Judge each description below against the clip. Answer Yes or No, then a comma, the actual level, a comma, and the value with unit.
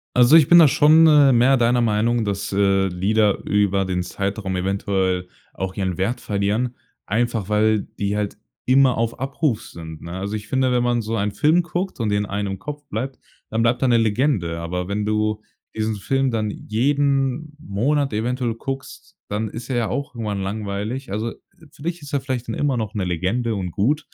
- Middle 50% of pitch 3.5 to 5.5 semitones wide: Yes, average, 4.7 semitones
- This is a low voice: Yes, low, 110 Hz